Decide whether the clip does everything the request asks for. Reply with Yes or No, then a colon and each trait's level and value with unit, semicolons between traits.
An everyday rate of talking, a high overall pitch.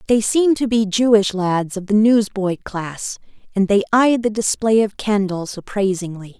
Yes: average, 170 wpm; high, 205 Hz